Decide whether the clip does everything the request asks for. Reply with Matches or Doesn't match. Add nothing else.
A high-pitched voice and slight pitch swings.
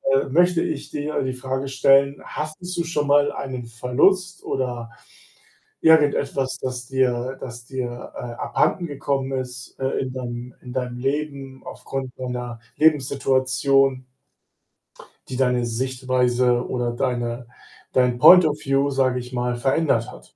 Doesn't match